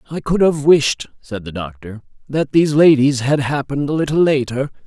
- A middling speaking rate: Yes, average, 185 wpm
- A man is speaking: Yes, male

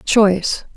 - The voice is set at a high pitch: Yes, high, 195 Hz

